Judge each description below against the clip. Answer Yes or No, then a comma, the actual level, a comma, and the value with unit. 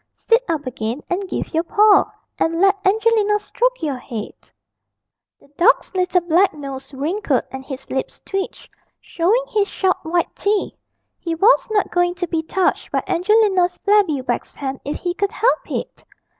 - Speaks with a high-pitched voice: Yes, very high, 360 Hz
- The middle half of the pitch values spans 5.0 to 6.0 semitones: Yes, wide, 5.5 semitones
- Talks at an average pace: Yes, average, 165 wpm